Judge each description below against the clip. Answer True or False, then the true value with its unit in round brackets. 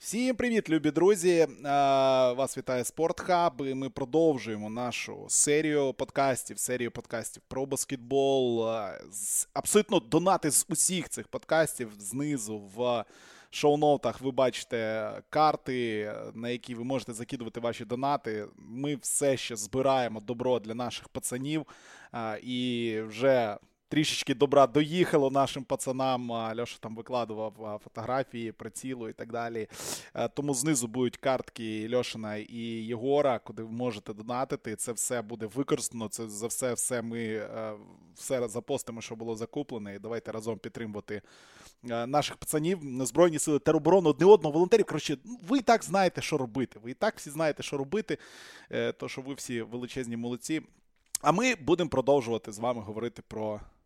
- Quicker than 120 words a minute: True (135 wpm)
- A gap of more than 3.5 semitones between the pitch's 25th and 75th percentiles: True (4.1 semitones)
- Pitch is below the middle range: True (130 Hz)